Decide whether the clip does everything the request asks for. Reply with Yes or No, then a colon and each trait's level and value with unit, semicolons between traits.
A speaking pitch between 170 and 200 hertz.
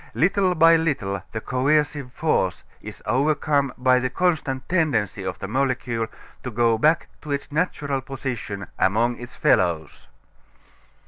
No: low, 130 Hz